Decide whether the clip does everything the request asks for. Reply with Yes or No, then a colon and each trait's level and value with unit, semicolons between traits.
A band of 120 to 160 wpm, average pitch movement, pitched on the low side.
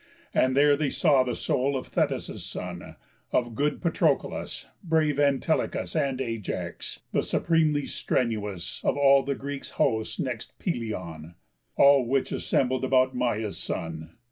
Yes: slow, 135 wpm; average, 3.8 semitones; low, 130 Hz